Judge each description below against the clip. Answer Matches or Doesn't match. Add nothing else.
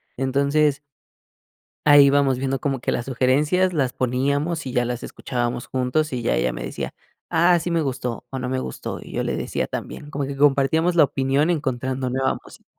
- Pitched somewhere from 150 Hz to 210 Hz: Doesn't match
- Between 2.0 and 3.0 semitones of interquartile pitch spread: Matches